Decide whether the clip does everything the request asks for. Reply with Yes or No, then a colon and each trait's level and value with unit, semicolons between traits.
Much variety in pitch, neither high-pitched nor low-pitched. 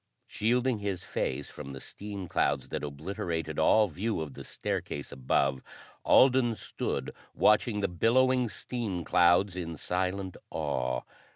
No: wide, 6.1 semitones; very low, 95 Hz